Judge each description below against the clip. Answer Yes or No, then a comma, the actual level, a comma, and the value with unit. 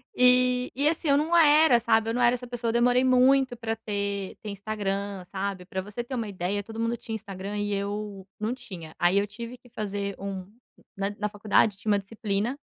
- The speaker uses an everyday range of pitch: Yes, average, 3.6 semitones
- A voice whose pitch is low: No, high, 215 Hz